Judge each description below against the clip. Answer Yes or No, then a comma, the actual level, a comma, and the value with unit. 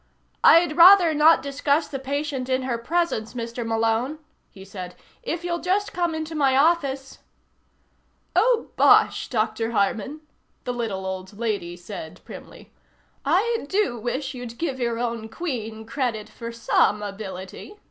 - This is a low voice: No, very high, 250 Hz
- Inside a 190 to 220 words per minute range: No, average, 145 wpm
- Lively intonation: Yes, wide, 6.0 semitones